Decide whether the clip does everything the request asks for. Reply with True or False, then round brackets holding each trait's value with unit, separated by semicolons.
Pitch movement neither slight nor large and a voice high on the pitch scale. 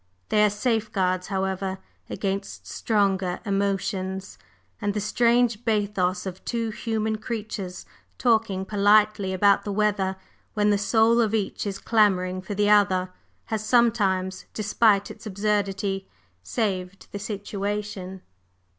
False (1.9 semitones; 205 Hz)